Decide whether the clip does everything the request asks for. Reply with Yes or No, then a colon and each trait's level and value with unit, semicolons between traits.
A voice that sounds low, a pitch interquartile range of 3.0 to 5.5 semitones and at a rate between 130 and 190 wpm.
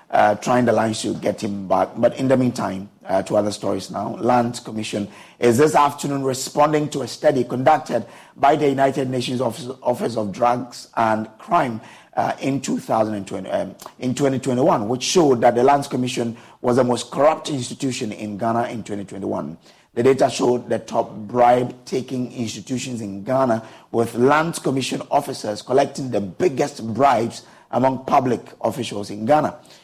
Yes: low, 125 Hz; average, 3.4 semitones; average, 165 wpm